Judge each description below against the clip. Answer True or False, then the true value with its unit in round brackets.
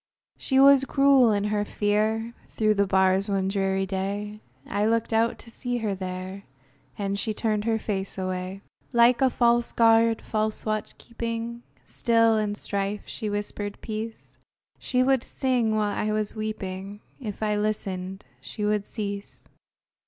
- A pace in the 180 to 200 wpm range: False (150 wpm)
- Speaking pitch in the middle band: False (215 Hz)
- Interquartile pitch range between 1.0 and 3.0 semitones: True (2.4 semitones)